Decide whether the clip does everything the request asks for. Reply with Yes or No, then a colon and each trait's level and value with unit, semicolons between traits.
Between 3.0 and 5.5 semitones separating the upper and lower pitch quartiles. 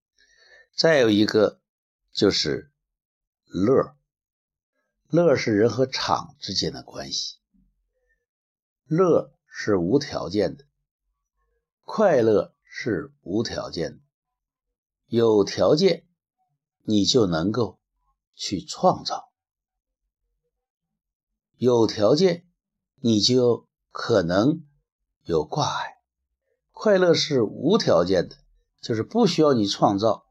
No: wide, 8.2 semitones